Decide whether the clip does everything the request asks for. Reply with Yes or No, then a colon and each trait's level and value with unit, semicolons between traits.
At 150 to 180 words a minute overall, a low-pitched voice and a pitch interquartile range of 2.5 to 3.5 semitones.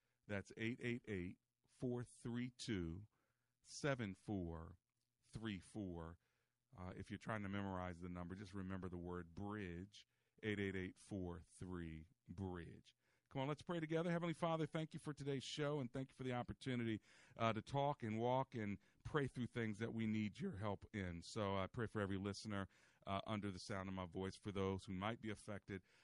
No: average, 160 wpm; low, 105 Hz; average, 4.2 semitones